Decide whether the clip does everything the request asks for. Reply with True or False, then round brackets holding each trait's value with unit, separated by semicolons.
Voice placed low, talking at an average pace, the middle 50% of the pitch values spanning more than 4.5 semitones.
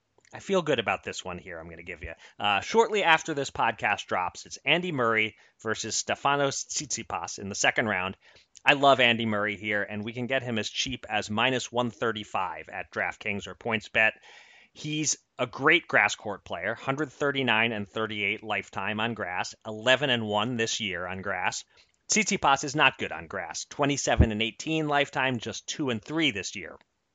True (120 Hz; 180 wpm; 5.1 semitones)